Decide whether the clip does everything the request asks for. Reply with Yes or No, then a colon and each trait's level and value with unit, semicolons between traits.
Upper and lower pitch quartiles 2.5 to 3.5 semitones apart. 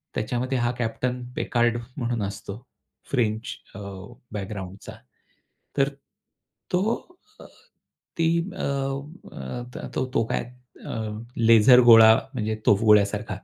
Yes: average, 3.0 semitones